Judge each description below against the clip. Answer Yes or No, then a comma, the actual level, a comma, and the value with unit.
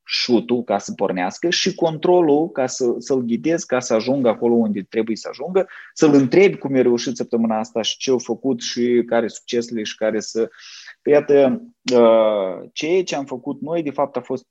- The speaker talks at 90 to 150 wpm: No, fast, 190 wpm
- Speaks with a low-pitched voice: Yes, low, 125 Hz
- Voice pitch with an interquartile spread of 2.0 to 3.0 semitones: No, average, 4.0 semitones